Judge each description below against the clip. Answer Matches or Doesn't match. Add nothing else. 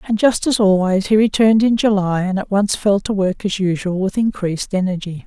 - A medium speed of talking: Doesn't match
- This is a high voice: Matches